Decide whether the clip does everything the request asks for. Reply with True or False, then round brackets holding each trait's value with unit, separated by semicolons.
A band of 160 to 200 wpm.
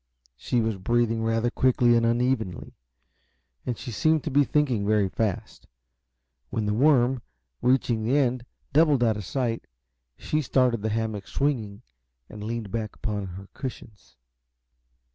False (145 wpm)